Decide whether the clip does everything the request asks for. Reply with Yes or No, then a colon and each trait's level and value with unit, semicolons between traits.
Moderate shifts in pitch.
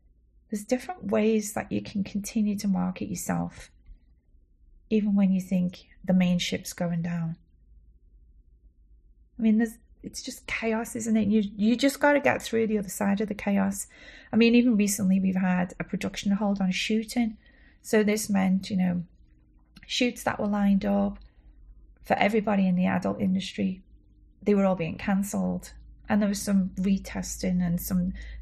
Yes: average, 3.9 semitones